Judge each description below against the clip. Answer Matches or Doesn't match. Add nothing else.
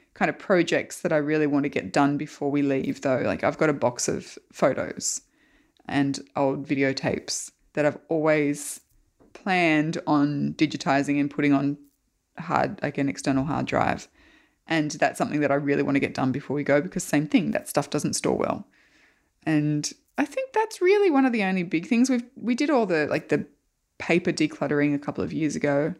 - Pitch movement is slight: Doesn't match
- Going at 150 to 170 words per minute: Doesn't match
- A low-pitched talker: Doesn't match